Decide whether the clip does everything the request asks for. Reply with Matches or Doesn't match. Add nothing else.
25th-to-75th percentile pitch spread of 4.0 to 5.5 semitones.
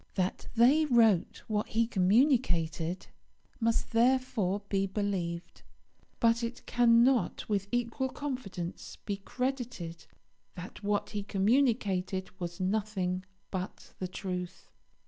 Matches